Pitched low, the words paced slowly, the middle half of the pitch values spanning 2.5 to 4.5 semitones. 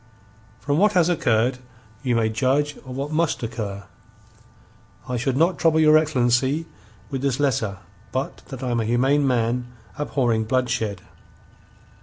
No: low, 130 Hz; average, 145 wpm; average, 3.8 semitones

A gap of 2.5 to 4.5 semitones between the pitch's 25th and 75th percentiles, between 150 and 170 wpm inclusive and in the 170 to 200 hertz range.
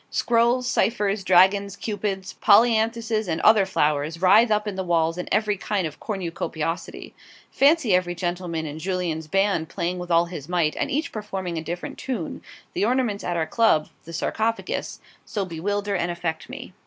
Yes: average, 4.1 semitones; average, 165 wpm; high, 190 Hz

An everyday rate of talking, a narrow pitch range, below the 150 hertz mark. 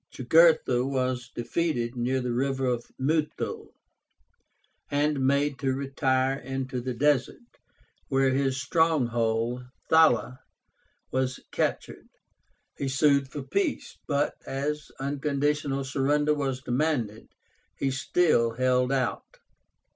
No: slow, 100 wpm; narrow, 2.3 semitones; low, 135 Hz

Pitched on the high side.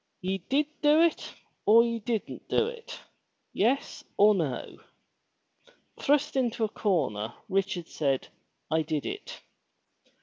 Yes: high, 215 Hz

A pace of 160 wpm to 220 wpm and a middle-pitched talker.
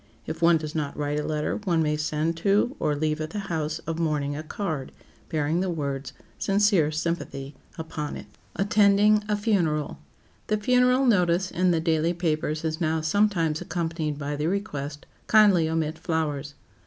Yes: average, 170 wpm; medium, 160 Hz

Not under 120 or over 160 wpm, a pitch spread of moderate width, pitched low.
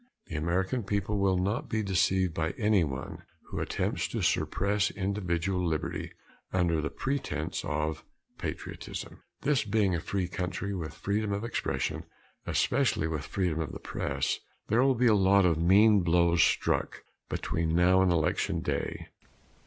Yes: average, 150 wpm; average, 3.4 semitones; very low, 95 Hz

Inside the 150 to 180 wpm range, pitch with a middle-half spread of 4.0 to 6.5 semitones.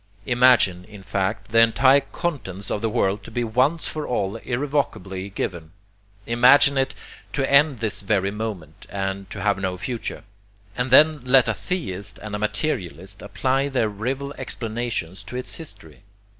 Yes: average, 155 wpm; average, 5.2 semitones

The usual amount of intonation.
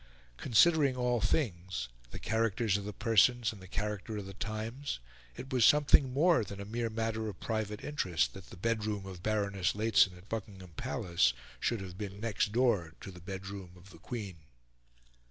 Yes: average, 3.2 semitones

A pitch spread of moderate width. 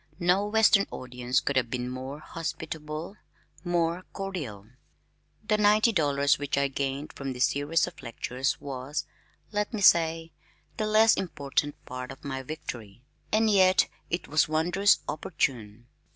No: wide, 5.9 semitones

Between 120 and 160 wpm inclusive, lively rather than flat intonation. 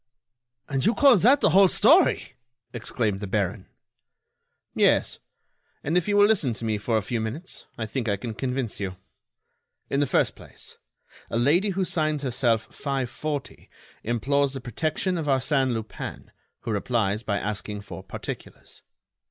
Yes: average, 155 wpm; wide, 5.7 semitones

